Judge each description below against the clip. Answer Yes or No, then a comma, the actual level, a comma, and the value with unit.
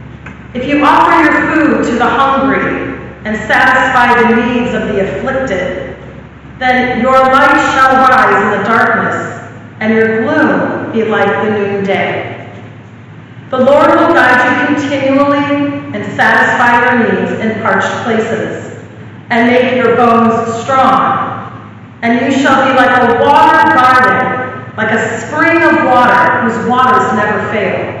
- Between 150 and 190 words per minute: No, average, 140 wpm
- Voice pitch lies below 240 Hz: No, high, 245 Hz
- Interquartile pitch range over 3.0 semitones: Yes, average, 3.5 semitones